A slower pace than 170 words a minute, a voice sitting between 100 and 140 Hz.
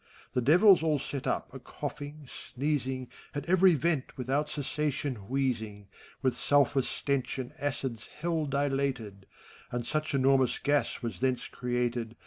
Yes: slow, 135 wpm; low, 135 Hz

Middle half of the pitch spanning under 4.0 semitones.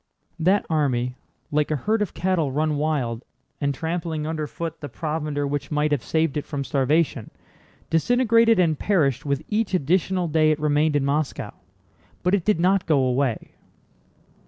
Yes: average, 3.2 semitones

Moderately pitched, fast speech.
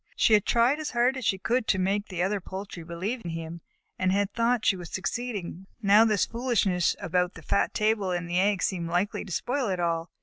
No: high, 195 Hz; fast, 230 wpm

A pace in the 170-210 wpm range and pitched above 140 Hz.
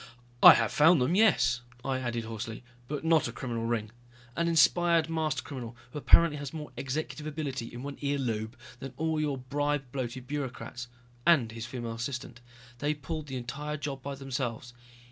No: average, 175 wpm; low, 135 Hz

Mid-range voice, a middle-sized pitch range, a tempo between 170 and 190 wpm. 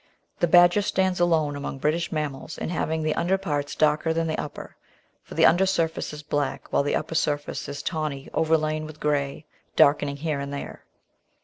No: medium, 155 Hz; narrow, 2.2 semitones; average, 185 wpm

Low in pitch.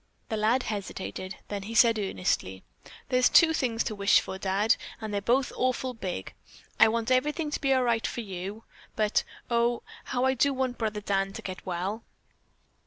No: high, 225 Hz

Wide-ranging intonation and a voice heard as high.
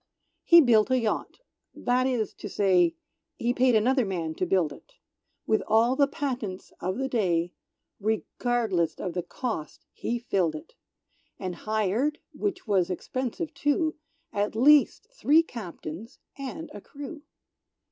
Yes: wide, 6.0 semitones; high, 225 Hz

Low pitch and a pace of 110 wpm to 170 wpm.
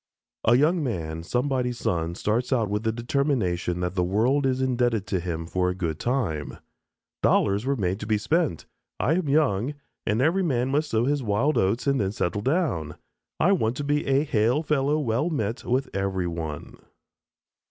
No: low, 120 Hz; average, 180 wpm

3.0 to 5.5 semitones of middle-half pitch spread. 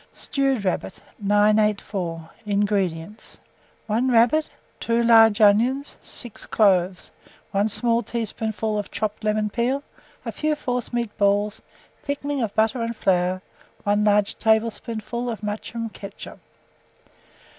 No: narrow, 2.4 semitones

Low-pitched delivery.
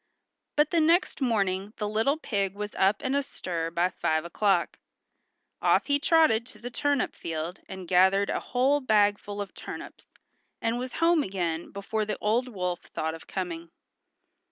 No: high, 205 Hz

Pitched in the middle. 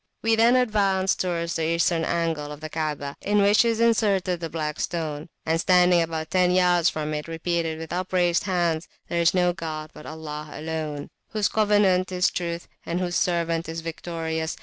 Yes: medium, 170 Hz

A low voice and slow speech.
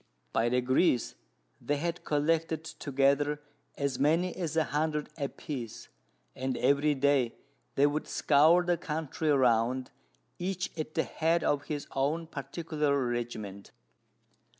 No: medium, 145 Hz; slow, 125 wpm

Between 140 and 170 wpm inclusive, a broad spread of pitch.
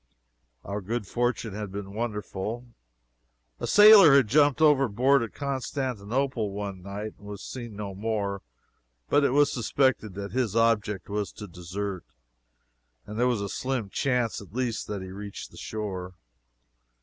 No: average, 150 wpm; average, 4.2 semitones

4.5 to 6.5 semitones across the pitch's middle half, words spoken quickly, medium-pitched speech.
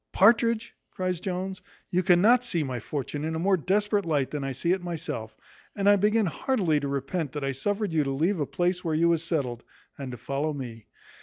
Yes: wide, 5.5 semitones; fast, 215 wpm; medium, 170 Hz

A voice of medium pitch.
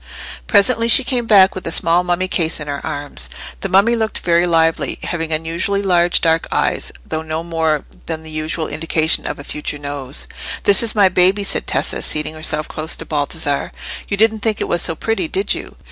Yes: medium, 165 Hz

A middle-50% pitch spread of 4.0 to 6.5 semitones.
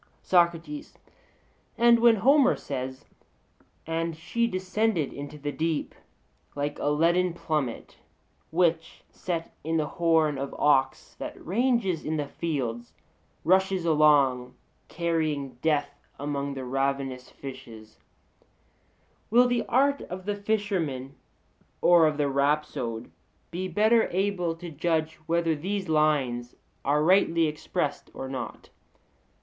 Yes: average, 4.6 semitones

